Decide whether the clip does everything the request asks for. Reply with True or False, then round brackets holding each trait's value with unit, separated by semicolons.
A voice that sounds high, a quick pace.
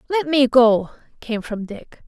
False (245 Hz; 175 wpm)